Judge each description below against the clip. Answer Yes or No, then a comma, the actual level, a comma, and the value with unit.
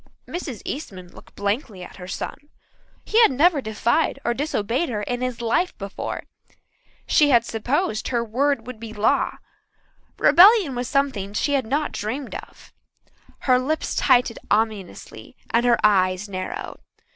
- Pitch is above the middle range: Yes, high, 240 Hz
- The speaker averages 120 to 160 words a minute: Yes, average, 145 wpm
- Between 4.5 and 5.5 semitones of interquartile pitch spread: Yes, average, 5.0 semitones